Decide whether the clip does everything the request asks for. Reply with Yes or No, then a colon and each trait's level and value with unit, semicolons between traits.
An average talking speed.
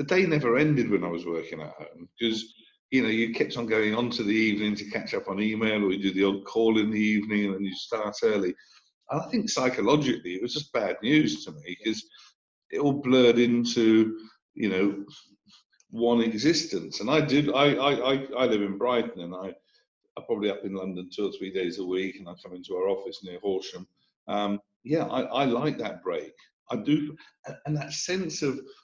No: fast, 215 wpm